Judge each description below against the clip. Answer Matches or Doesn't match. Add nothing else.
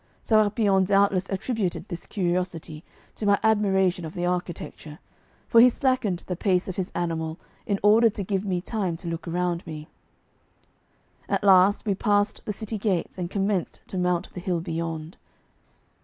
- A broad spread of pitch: Doesn't match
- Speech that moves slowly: Doesn't match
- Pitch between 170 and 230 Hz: Matches